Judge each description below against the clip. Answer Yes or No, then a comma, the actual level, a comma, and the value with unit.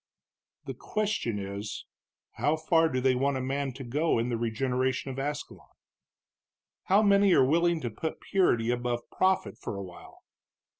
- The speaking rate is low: No, average, 160 wpm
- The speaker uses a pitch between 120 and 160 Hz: Yes, low, 135 Hz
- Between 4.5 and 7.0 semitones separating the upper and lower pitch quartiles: Yes, average, 5.3 semitones